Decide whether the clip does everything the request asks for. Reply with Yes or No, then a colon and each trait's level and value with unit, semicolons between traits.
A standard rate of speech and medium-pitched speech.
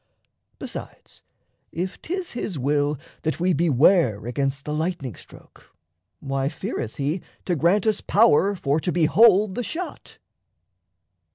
No: slow, 125 wpm; medium, 165 Hz